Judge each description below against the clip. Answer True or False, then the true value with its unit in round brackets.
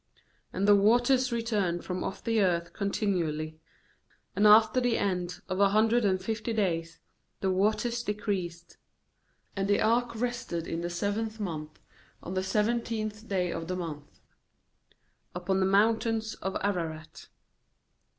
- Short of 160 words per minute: True (140 wpm)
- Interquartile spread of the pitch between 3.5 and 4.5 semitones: True (4.0 semitones)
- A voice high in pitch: True (200 Hz)